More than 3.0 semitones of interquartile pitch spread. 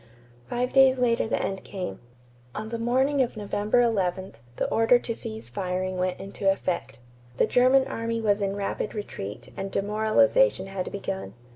Yes: average, 4.1 semitones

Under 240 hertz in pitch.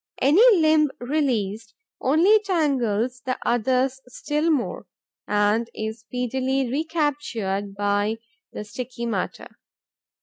No: very high, 250 Hz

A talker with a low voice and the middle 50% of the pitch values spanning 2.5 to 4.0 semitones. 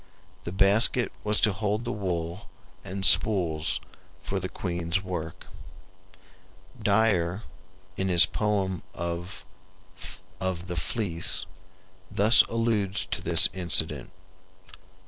Yes: very low, 95 Hz; average, 3.3 semitones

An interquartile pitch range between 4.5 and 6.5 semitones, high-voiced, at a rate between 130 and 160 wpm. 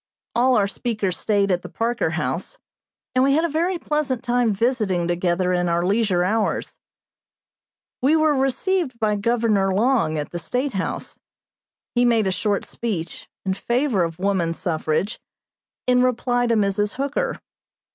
Yes: average, 5.1 semitones; high, 220 Hz; average, 155 wpm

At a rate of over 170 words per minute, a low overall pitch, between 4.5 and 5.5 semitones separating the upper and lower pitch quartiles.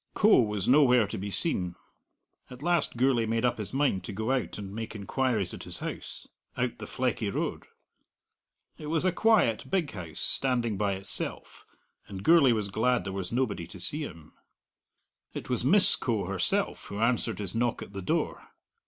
Yes: average, 180 wpm; low, 115 Hz; average, 4.8 semitones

